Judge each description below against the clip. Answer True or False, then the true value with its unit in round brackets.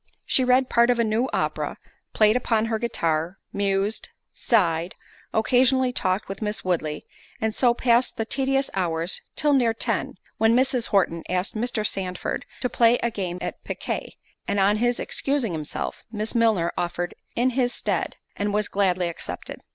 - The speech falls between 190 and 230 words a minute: False (165 wpm)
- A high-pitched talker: True (220 Hz)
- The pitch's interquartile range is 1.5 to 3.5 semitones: False (4.6 semitones)